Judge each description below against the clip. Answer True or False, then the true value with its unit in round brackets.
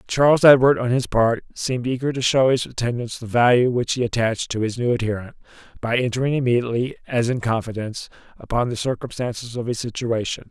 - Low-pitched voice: True (120 Hz)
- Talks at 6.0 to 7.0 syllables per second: True (6.2 syllables/s)